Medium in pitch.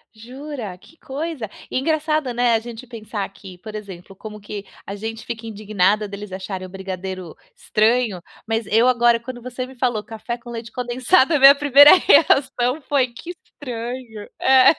No: high, 235 Hz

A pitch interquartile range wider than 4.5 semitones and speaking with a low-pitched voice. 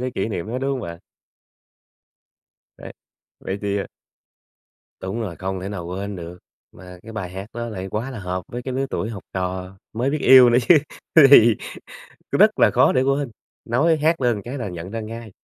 Yes: average, 5.1 semitones; low, 110 Hz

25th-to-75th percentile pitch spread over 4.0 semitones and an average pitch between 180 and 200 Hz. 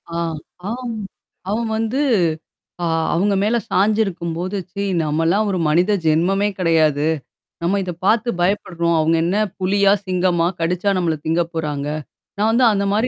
No: average, 3.7 semitones; medium, 185 Hz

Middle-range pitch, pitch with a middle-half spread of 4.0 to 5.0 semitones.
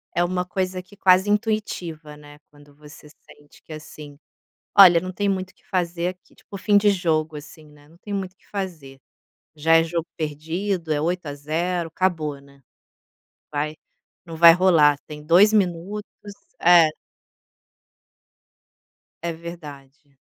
No: medium, 170 Hz; average, 3.5 semitones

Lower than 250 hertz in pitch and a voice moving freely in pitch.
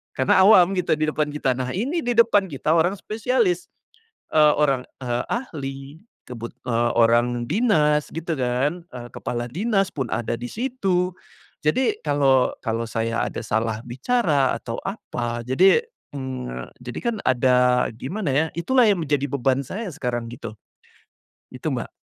Yes: medium, 140 Hz; wide, 7.1 semitones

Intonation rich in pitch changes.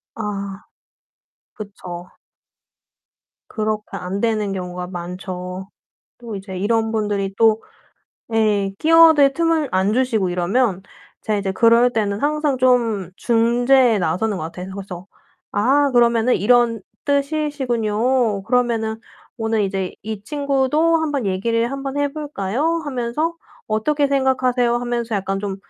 No: average, 4.8 semitones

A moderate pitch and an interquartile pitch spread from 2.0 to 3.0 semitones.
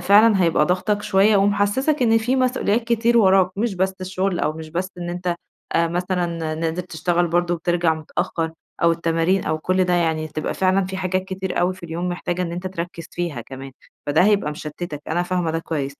Yes: medium, 175 Hz; narrow, 2.6 semitones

